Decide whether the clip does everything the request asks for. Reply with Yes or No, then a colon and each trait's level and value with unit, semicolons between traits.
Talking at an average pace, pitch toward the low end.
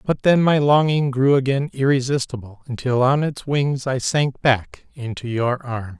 Yes: average, 170 wpm; low, 130 Hz